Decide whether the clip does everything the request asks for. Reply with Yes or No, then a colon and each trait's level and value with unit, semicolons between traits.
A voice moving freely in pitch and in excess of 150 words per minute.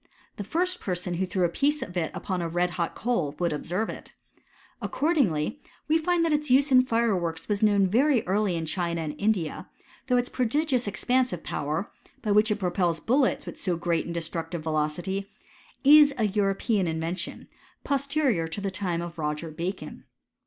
Yes: wide, 6.7 semitones; average, 185 wpm